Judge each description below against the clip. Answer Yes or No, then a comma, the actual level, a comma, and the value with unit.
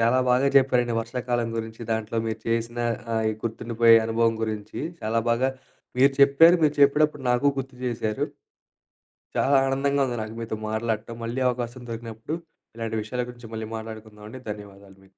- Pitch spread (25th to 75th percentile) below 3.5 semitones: Yes, narrow, 2.4 semitones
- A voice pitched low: Yes, low, 115 Hz